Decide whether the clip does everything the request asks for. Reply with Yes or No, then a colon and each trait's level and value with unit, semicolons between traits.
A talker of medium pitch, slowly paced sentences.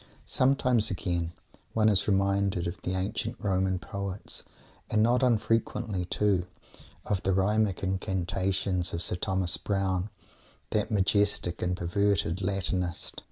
No: very low, 95 Hz; slow, 120 wpm